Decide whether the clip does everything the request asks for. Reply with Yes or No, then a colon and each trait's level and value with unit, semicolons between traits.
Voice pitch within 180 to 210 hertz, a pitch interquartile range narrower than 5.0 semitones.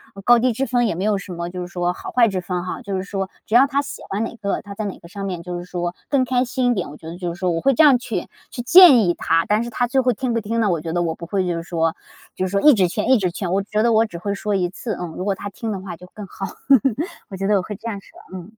Yes: high, 200 Hz; average, 4.5 semitones